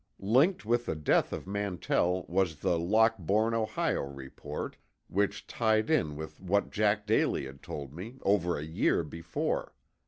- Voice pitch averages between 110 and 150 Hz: No, very low, 95 Hz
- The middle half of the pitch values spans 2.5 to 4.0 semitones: No, average, 5.3 semitones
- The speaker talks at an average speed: Yes, average, 150 wpm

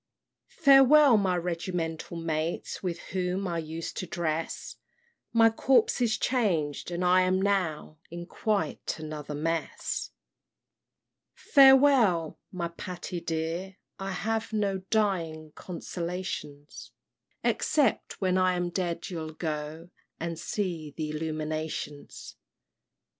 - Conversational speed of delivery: No, slow, 110 wpm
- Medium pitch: Yes, medium, 175 Hz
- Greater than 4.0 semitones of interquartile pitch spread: No, average, 3.5 semitones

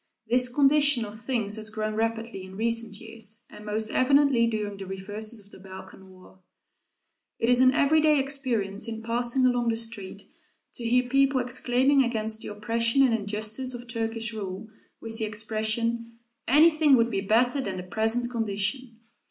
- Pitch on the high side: Yes, high, 230 Hz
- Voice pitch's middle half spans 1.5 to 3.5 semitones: Yes, average, 2.7 semitones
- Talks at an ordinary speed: Yes, average, 165 wpm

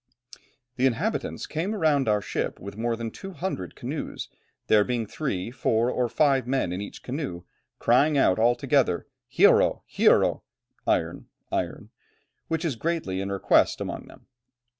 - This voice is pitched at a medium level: No, low, 125 Hz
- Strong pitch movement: Yes, wide, 6.2 semitones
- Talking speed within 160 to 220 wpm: No, average, 145 wpm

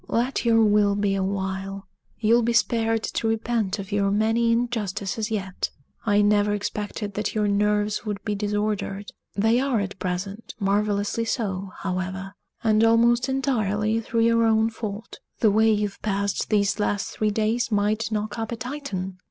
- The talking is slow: No, average, 160 wpm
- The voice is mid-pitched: No, high, 210 Hz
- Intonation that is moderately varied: No, narrow, 2.1 semitones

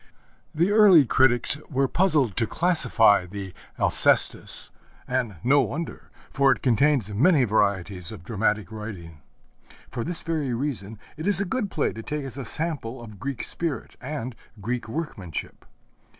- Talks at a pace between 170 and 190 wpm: No, average, 150 wpm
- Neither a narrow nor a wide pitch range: No, wide, 6.0 semitones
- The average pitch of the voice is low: Yes, low, 125 Hz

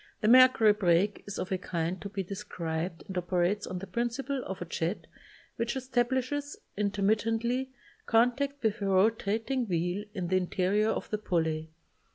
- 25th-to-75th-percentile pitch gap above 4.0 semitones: Yes, average, 4.5 semitones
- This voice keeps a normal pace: Yes, average, 160 wpm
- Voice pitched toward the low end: No, high, 205 Hz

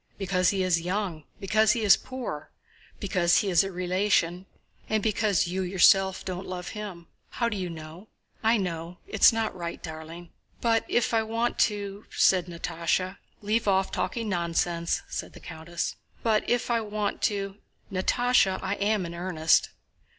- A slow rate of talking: No, average, 165 wpm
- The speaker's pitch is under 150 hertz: No, high, 190 Hz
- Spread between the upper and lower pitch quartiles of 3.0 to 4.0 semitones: Yes, average, 3.5 semitones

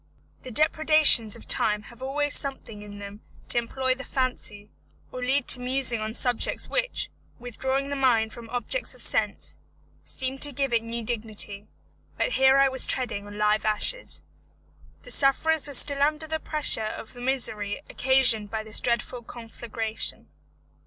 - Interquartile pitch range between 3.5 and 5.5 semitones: Yes, average, 3.8 semitones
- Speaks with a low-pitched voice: No, high, 245 Hz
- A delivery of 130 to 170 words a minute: Yes, average, 160 wpm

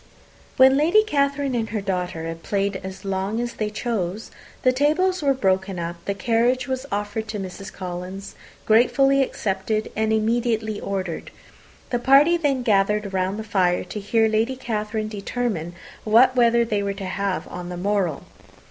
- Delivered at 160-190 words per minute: Yes, average, 165 wpm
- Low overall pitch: No, high, 215 Hz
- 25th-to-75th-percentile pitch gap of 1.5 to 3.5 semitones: No, average, 4.2 semitones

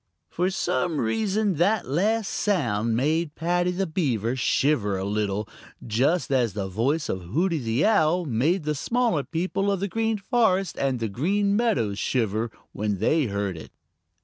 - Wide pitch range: Yes, wide, 9.0 semitones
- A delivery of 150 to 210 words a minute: Yes, average, 160 wpm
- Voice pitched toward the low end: No, medium, 150 Hz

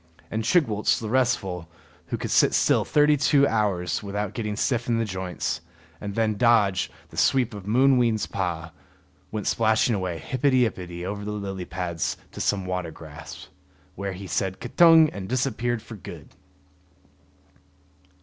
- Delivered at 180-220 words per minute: No, average, 150 wpm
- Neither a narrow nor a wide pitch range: Yes, average, 4.6 semitones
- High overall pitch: No, low, 105 Hz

